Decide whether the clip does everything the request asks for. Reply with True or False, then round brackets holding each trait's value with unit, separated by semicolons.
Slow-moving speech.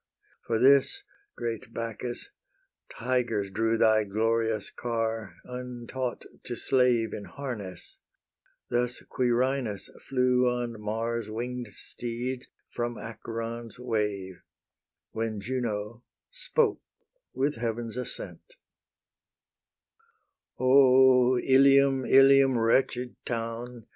True (90 wpm)